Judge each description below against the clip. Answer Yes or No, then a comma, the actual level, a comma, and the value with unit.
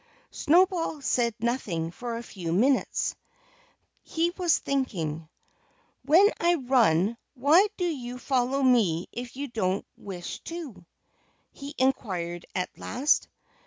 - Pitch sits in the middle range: No, high, 245 Hz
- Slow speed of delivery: Yes, slow, 120 wpm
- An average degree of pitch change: No, wide, 7.1 semitones